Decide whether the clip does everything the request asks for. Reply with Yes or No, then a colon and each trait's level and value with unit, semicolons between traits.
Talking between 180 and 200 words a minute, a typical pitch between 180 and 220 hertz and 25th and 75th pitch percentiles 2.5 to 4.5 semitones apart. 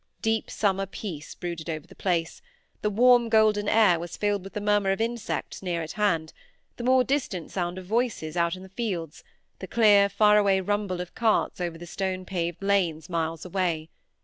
Yes: average, 185 wpm; high, 190 Hz; average, 3.5 semitones